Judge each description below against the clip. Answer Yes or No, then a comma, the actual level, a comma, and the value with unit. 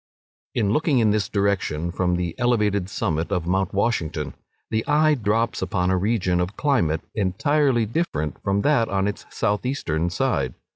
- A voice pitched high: No, low, 100 Hz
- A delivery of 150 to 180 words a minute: Yes, average, 160 wpm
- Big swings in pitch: No, average, 4.7 semitones